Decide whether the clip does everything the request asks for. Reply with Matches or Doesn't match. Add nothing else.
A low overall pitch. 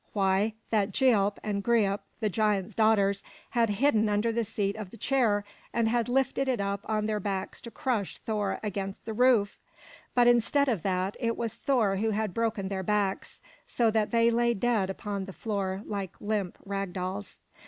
Doesn't match